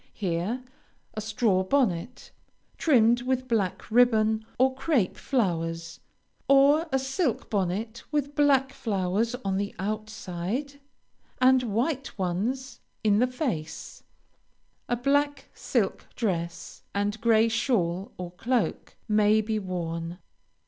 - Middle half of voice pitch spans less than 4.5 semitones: No, wide, 5.5 semitones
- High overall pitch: Yes, high, 220 Hz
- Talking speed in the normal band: No, slow, 115 wpm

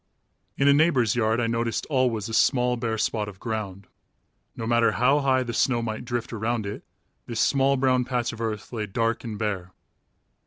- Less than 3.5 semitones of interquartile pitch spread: Yes, narrow, 2.4 semitones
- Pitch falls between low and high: No, low, 115 Hz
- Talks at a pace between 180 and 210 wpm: Yes, average, 190 wpm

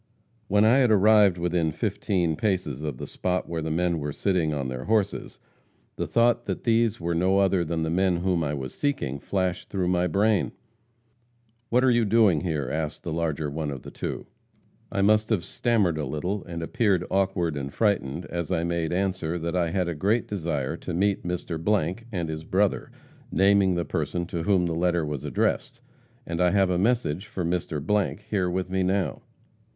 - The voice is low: Yes, very low, 90 Hz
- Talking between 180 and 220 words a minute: Yes, average, 190 wpm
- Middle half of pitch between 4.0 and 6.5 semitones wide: No, average, 3.5 semitones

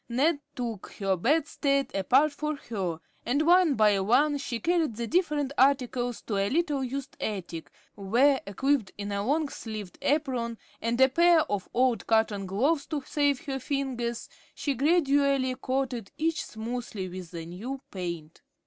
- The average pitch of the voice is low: No, very high, 255 Hz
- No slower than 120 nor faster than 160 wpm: Yes, average, 155 wpm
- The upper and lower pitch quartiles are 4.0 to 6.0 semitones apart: Yes, wide, 5.4 semitones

